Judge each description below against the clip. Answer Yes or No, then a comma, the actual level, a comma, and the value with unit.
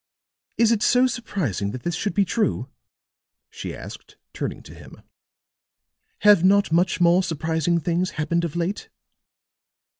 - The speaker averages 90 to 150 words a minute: Yes, average, 140 wpm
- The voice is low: No, medium, 175 Hz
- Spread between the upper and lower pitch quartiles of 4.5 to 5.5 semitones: No, average, 3.6 semitones